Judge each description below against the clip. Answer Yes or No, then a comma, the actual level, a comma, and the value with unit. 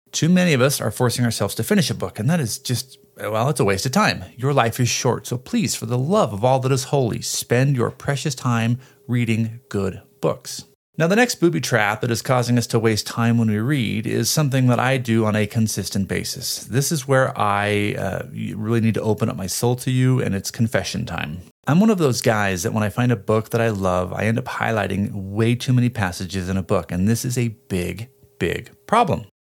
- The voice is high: No, low, 115 Hz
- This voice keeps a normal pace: No, fast, 235 wpm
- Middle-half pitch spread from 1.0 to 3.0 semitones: No, average, 3.7 semitones